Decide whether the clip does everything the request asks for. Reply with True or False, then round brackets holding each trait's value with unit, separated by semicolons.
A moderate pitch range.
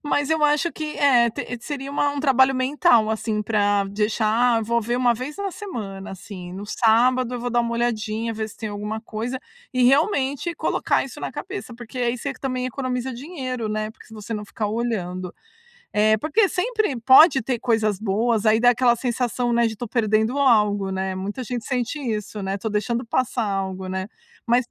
True (3.2 semitones)